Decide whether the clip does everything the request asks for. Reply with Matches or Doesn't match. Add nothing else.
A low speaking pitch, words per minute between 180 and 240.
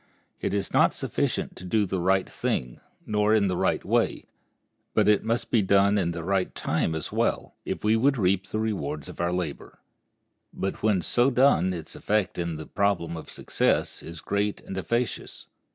Matches